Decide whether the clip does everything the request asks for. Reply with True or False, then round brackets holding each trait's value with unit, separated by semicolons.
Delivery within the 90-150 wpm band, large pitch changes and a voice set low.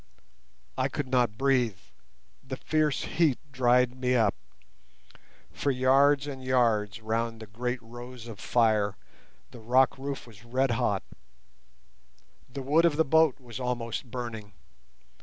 False (135 wpm; 2.7 semitones; 125 Hz)